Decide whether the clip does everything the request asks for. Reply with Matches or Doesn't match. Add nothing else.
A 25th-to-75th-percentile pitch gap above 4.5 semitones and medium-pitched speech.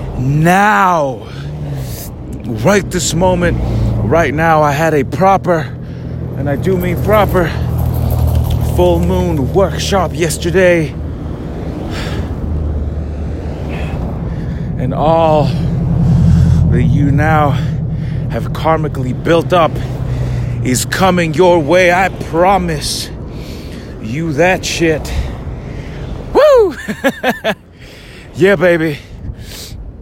Matches